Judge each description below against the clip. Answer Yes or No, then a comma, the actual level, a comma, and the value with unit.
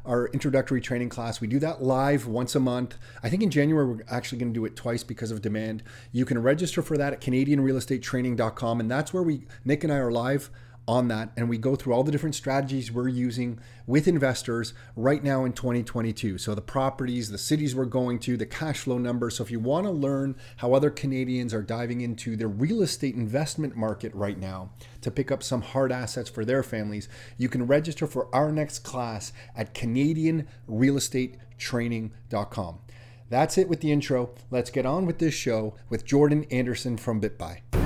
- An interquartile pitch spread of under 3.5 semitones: Yes, average, 2.8 semitones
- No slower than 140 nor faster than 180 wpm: No, average, 195 wpm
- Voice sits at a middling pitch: No, low, 125 Hz